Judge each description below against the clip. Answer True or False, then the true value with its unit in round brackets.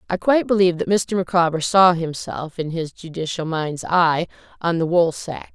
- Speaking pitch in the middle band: True (170 Hz)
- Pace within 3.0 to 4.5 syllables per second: False (5.0 syllables/s)